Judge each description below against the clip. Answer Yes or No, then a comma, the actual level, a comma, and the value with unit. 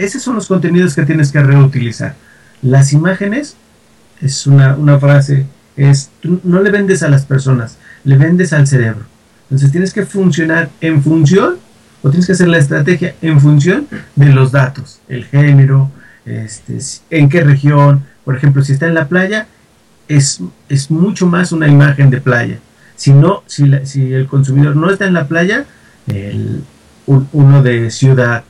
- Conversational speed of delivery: Yes, average, 170 wpm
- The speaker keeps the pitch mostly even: No, average, 3.8 semitones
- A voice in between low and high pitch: Yes, medium, 145 Hz